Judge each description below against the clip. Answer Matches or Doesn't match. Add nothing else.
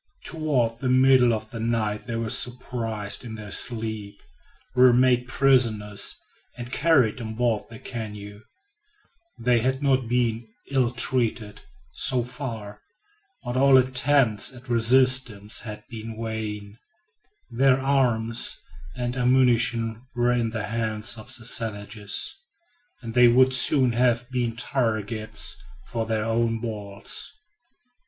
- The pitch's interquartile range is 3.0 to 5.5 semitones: Doesn't match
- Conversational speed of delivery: Doesn't match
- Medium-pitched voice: Doesn't match